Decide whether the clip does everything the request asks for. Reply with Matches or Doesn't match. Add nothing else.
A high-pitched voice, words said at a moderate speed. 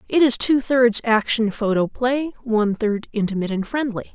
Matches